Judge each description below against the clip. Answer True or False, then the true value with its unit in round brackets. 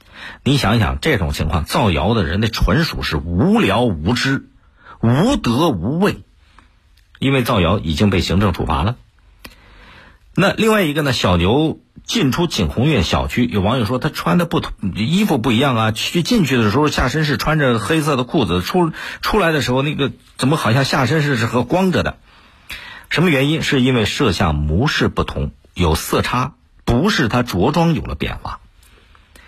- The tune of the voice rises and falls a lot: True (8.0 semitones)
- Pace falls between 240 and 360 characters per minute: True (260 characters per minute)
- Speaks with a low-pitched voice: True (115 Hz)